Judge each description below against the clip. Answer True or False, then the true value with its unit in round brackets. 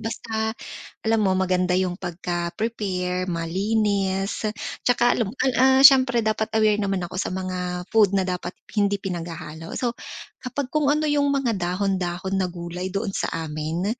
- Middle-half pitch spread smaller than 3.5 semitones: False (3.8 semitones)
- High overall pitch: True (195 Hz)